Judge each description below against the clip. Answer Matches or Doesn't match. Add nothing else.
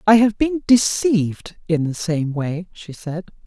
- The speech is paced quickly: Doesn't match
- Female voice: Matches